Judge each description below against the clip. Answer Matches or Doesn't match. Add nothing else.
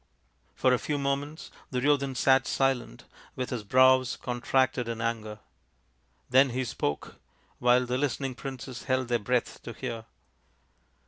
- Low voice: Matches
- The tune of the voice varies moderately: Doesn't match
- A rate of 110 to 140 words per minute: Matches